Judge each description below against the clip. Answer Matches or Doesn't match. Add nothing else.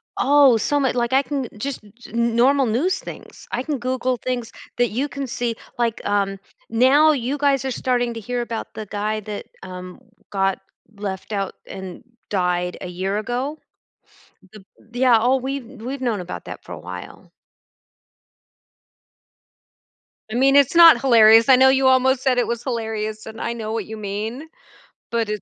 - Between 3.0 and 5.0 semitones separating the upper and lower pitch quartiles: Matches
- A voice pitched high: Matches